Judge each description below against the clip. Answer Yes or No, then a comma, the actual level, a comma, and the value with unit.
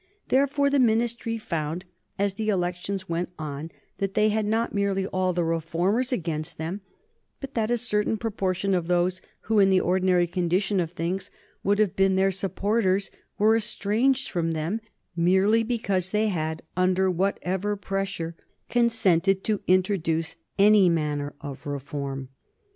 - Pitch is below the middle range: No, high, 190 Hz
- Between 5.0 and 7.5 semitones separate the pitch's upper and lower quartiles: No, average, 3.6 semitones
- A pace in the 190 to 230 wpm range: No, average, 150 wpm